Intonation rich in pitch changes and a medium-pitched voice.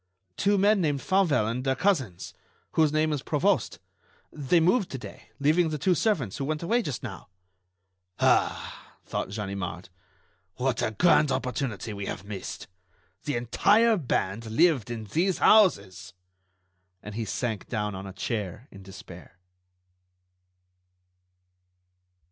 No: wide, 8.3 semitones; low, 130 Hz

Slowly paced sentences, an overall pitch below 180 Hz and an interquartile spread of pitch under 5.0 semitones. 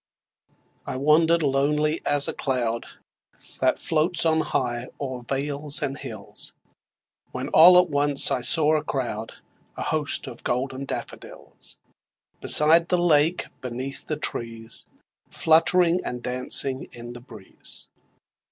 Yes: slow, 125 wpm; medium, 140 Hz; average, 4.0 semitones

